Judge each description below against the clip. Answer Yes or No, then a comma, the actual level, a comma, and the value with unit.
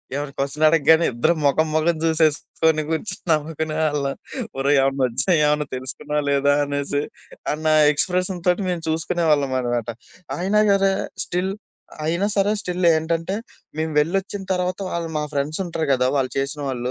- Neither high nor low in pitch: Yes, medium, 155 Hz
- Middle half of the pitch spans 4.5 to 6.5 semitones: No, average, 3.4 semitones